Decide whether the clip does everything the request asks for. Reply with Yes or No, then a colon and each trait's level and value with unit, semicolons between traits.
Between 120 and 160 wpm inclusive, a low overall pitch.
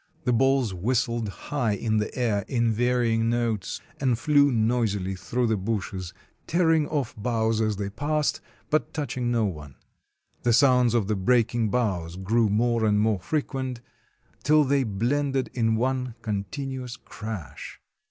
Yes: average, 150 wpm; low, 115 Hz